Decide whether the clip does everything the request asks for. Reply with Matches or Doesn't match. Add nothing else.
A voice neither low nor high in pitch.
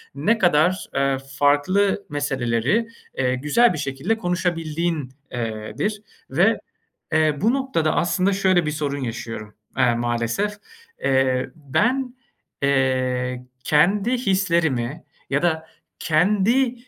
Matches